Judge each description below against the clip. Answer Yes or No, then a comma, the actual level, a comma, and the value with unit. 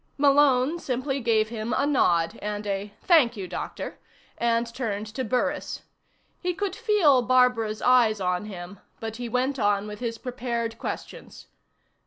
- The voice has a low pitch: No, high, 235 Hz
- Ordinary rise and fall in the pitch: Yes, average, 4.0 semitones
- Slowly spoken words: No, average, 155 wpm